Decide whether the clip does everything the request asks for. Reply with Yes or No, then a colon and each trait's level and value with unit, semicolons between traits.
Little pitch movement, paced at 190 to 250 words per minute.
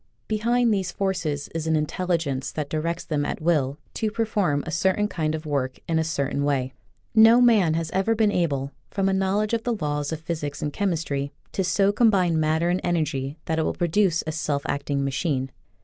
No: average, 4.9 semitones; average, 200 wpm